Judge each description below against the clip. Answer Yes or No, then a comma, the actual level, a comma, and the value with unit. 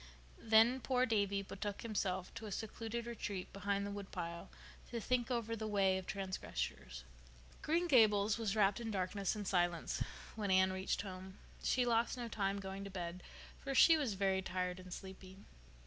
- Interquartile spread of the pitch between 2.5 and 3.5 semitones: Yes, average, 3.2 semitones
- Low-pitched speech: No, high, 200 Hz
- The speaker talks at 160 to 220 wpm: Yes, average, 170 wpm